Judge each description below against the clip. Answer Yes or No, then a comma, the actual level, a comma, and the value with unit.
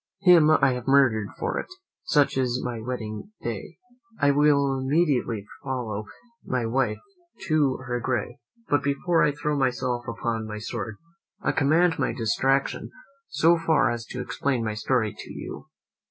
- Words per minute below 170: Yes, average, 155 wpm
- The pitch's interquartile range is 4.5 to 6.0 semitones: No, average, 3.7 semitones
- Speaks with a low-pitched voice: Yes, low, 130 Hz